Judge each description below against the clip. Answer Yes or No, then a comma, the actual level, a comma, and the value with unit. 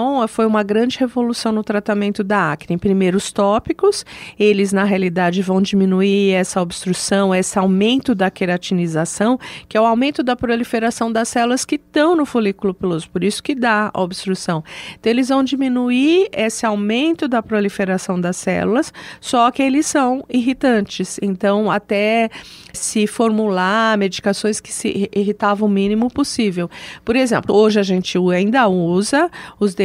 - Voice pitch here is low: No, high, 210 Hz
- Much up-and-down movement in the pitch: No, average, 3.8 semitones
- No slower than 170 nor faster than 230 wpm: No, average, 150 wpm